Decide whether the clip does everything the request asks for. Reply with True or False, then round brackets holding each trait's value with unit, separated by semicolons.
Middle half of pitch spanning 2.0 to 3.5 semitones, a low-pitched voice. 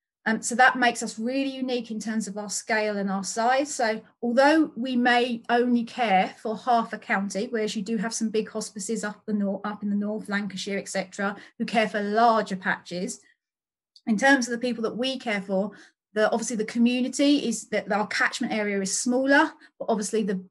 False (2.6 semitones; 220 Hz)